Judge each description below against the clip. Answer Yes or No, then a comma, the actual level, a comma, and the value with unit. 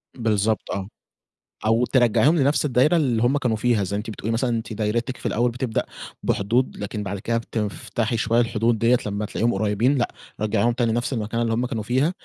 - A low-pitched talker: Yes, low, 115 Hz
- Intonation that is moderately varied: No, narrow, 2.3 semitones